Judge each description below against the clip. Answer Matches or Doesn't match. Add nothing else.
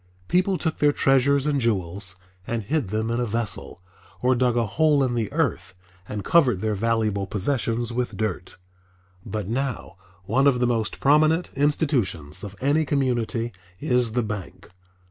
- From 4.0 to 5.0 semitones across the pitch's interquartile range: Matches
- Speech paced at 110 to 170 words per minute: Matches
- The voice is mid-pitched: Doesn't match